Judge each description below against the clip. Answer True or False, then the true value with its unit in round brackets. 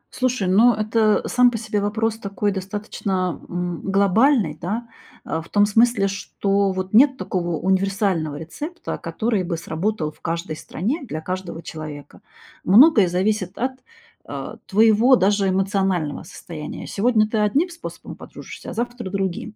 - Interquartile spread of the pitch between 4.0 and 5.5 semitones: False (3.6 semitones)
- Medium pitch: False (200 Hz)